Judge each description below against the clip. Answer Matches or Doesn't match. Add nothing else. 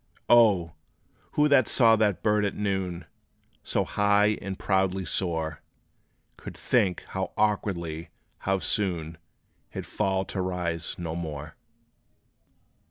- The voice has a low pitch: Matches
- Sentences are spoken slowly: Matches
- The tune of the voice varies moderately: Matches